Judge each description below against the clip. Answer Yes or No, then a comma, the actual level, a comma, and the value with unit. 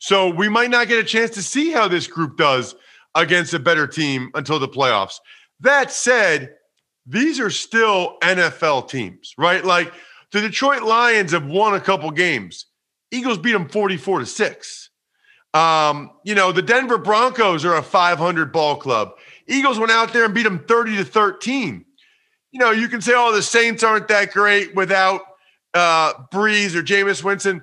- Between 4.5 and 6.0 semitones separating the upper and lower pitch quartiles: Yes, average, 4.8 semitones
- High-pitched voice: Yes, high, 205 Hz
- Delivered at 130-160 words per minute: No, average, 175 wpm